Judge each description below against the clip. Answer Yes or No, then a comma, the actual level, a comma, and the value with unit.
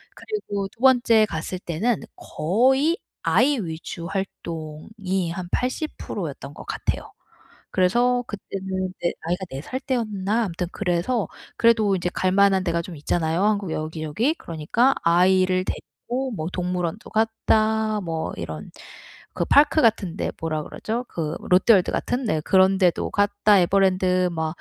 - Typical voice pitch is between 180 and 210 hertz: Yes, high, 190 Hz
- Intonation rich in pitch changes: No, average, 4.5 semitones